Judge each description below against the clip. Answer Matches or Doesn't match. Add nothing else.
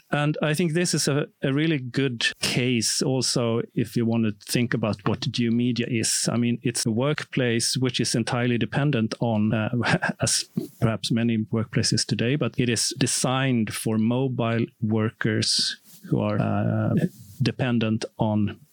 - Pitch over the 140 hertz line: Doesn't match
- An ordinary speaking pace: Matches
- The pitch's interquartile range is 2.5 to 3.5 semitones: Matches